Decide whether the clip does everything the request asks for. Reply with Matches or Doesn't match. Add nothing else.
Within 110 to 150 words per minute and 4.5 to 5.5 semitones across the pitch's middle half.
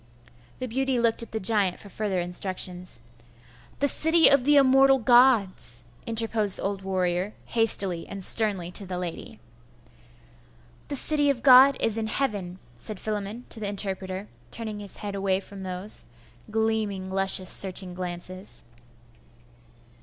Doesn't match